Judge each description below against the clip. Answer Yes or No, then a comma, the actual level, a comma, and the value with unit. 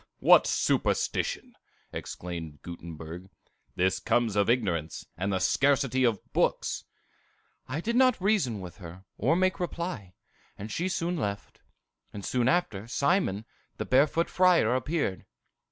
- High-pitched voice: No, low, 120 Hz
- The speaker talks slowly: Yes, slow, 130 wpm